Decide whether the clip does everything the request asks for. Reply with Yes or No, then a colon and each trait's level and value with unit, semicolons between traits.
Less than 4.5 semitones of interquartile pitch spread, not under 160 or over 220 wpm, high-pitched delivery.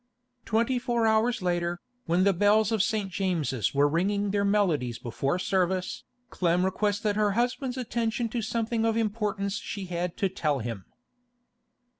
No: average, 4.1 semitones; average, 150 wpm; high, 200 Hz